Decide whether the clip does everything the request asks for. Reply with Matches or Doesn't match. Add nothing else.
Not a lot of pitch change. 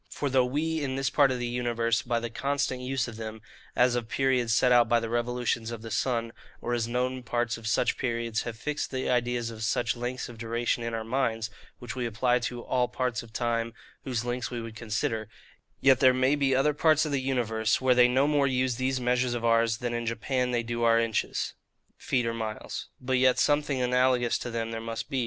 Matches